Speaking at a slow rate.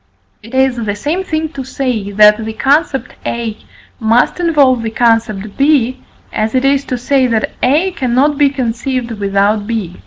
No: average, 165 wpm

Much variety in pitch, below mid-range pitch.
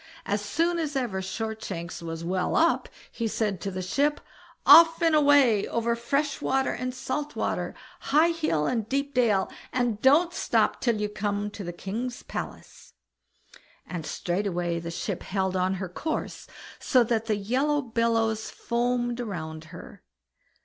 No: wide, 5.9 semitones; high, 225 Hz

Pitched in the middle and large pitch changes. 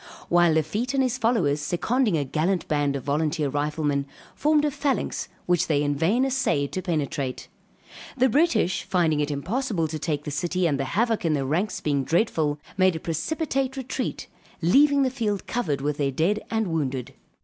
Yes: medium, 170 Hz; wide, 8.0 semitones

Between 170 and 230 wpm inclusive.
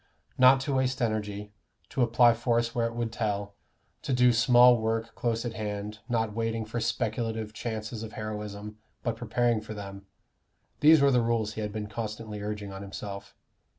Yes: average, 175 wpm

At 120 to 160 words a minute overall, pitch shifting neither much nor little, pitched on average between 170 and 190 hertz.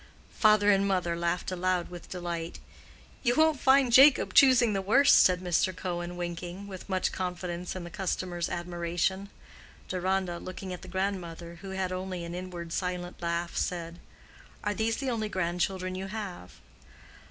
No: average, 155 wpm; narrow, 2.2 semitones; medium, 185 Hz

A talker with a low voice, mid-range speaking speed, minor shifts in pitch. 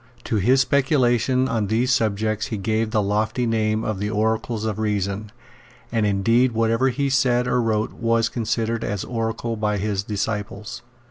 Yes: low, 110 Hz; average, 160 wpm; narrow, 2.1 semitones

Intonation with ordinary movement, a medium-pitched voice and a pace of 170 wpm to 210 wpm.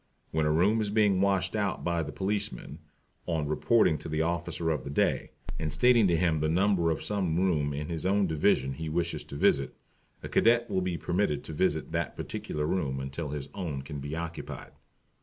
No: average, 4.1 semitones; very low, 85 Hz; average, 200 wpm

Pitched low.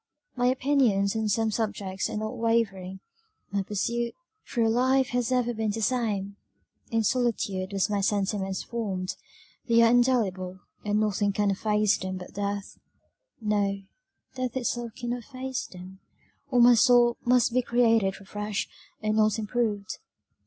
No: high, 215 Hz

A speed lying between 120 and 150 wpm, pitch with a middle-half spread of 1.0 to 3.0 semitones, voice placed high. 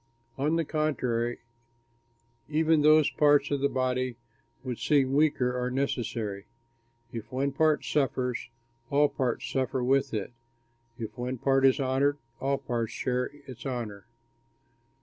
No: slow, 135 wpm; narrow, 2.5 semitones; low, 130 Hz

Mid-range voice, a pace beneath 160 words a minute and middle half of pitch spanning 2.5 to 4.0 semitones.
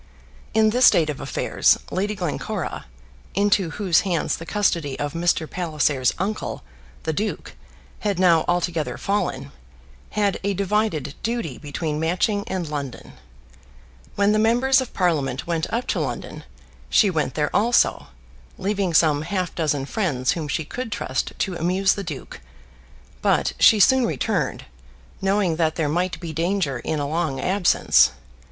No: medium, 175 Hz; average, 145 wpm; average, 4.8 semitones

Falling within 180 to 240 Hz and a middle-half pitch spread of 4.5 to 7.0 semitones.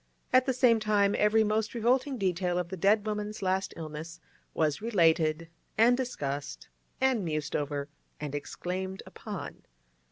Yes: high, 190 Hz; wide, 5.5 semitones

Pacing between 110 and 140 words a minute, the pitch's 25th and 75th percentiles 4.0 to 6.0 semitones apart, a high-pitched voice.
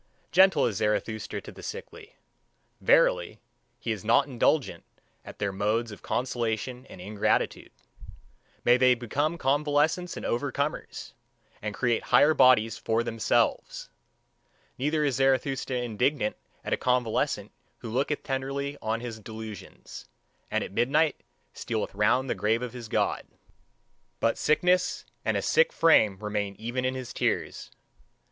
No: slow, 135 wpm; average, 4.5 semitones; low, 125 Hz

